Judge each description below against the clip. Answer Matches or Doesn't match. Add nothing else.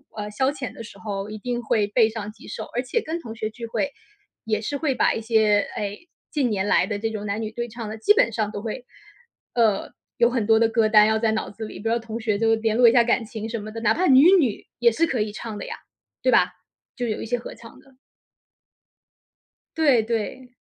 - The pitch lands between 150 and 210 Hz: Doesn't match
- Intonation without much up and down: Matches